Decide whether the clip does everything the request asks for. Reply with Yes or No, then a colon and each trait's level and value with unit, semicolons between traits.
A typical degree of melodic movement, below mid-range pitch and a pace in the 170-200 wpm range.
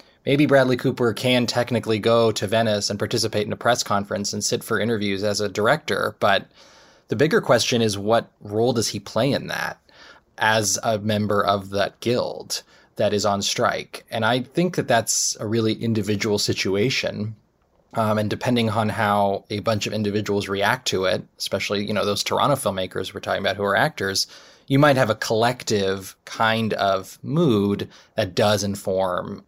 No: narrow, 2.3 semitones; low, 110 Hz; average, 175 wpm